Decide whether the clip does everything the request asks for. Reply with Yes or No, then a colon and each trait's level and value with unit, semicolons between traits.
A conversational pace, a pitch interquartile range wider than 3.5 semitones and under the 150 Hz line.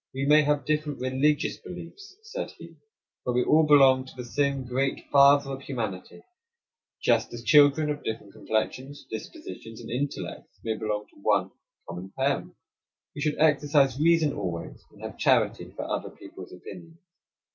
Yes: average, 155 wpm; average, 3.9 semitones; low, 135 Hz